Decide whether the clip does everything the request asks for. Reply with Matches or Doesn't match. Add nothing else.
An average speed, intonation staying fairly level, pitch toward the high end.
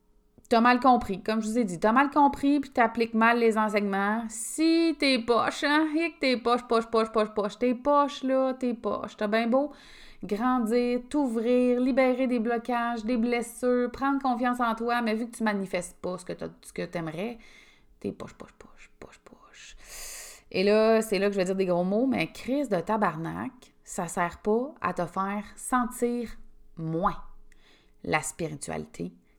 Doesn't match